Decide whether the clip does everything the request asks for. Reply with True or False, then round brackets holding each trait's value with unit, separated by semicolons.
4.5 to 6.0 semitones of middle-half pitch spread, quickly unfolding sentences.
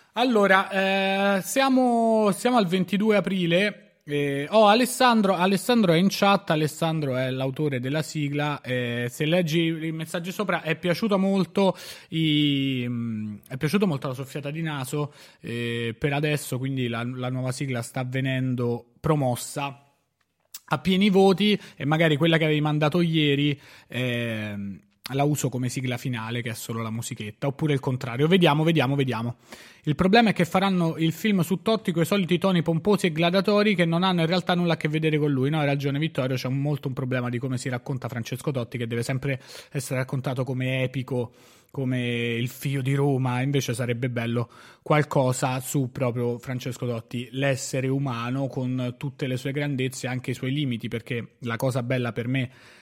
True (4.9 semitones; 175 wpm)